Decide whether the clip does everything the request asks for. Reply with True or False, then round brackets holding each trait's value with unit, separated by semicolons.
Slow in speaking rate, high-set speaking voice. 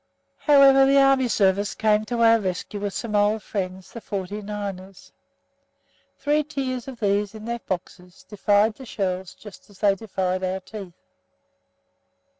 False (150 wpm; 210 Hz)